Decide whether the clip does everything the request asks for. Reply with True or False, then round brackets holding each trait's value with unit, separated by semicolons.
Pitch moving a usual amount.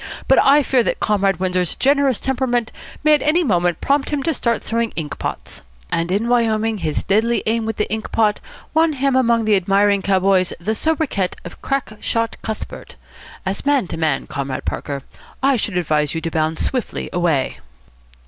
False (6.2 semitones)